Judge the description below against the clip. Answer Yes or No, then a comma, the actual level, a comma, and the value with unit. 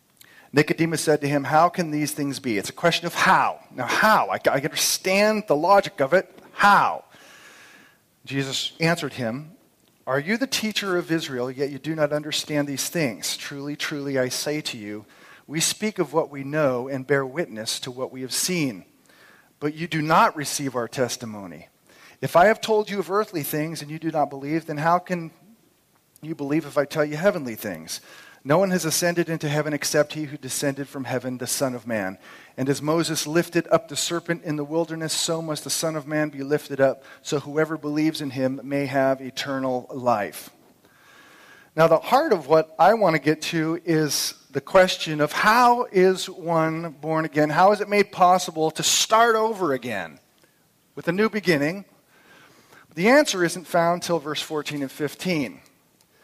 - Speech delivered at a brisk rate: No, average, 185 wpm